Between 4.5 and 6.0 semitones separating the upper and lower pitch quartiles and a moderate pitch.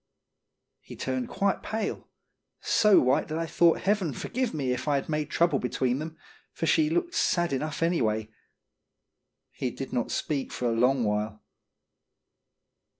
Yes: wide, 5.5 semitones; medium, 150 Hz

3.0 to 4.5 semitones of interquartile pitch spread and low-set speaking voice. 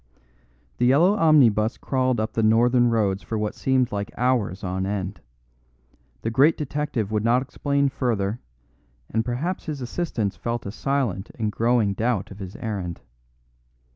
Yes: average, 3.9 semitones; low, 115 Hz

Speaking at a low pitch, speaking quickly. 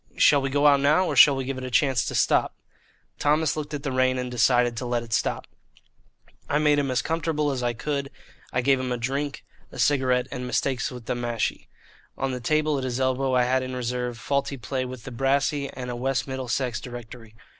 Yes: low, 130 Hz; fast, 220 wpm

